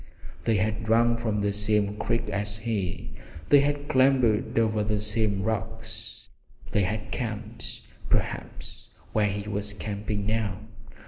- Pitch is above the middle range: No, low, 110 Hz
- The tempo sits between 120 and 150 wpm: Yes, slow, 135 wpm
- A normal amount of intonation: No, narrow, 1.5 semitones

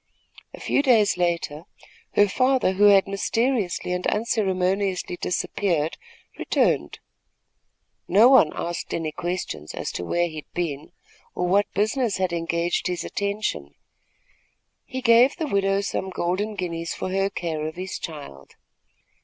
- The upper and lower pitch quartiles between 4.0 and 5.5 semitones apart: No, average, 3.3 semitones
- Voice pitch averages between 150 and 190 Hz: Yes, medium, 185 Hz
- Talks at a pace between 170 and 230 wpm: No, slow, 135 wpm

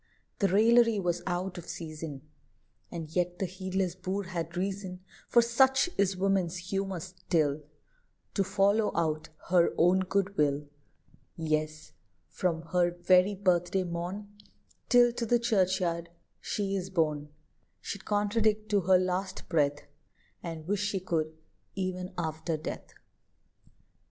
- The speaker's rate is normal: No, slow, 130 wpm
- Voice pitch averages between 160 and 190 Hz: Yes, medium, 185 Hz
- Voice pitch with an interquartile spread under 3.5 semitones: Yes, average, 2.8 semitones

